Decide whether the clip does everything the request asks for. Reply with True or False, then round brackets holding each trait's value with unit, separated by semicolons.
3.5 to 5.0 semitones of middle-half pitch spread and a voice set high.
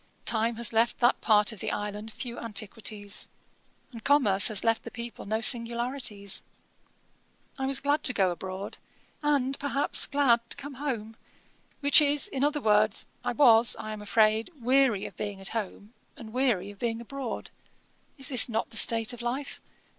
True (3.9 semitones; 230 Hz)